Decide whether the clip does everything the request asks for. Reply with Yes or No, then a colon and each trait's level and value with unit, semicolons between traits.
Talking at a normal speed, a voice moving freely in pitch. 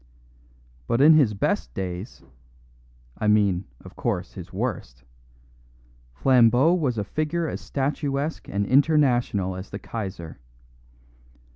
No: slow, 115 wpm; wide, 6.9 semitones